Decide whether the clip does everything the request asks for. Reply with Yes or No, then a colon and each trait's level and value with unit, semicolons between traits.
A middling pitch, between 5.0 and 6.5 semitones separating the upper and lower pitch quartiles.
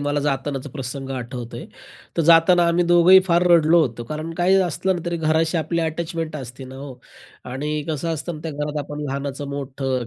No: medium, 150 Hz; average, 3.7 semitones